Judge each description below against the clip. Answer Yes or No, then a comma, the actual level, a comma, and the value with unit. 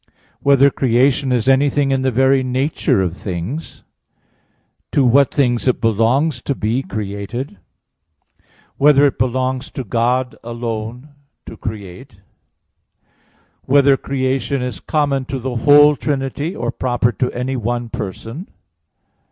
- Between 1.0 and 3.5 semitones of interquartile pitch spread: Yes, average, 2.9 semitones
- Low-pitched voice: Yes, low, 130 Hz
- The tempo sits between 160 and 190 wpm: No, slow, 135 wpm